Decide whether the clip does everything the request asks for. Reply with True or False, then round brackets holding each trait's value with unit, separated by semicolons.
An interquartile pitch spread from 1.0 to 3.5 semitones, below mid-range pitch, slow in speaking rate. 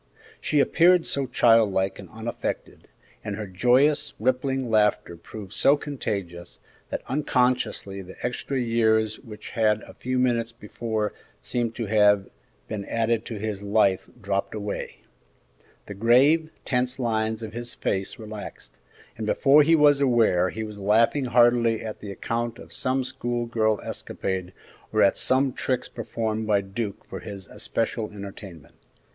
False (3.2 semitones; 110 Hz; 145 wpm)